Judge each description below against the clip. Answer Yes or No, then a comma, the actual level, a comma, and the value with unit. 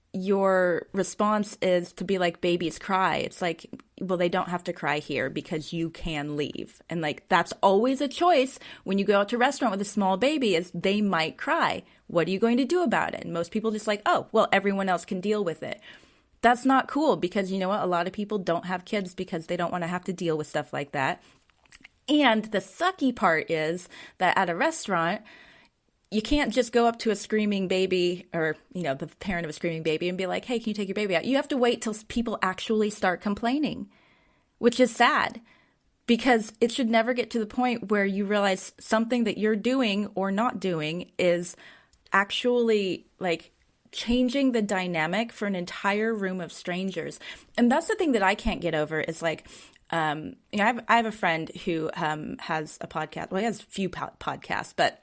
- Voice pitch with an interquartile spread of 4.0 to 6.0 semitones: Yes, average, 4.7 semitones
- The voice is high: Yes, high, 195 Hz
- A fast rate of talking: Yes, fast, 220 wpm